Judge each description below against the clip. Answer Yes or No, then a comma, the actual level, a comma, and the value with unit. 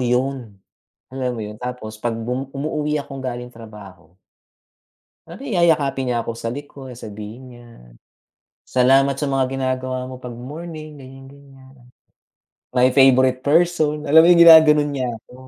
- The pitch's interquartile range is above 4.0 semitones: No, average, 2.8 semitones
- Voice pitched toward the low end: Yes, low, 130 Hz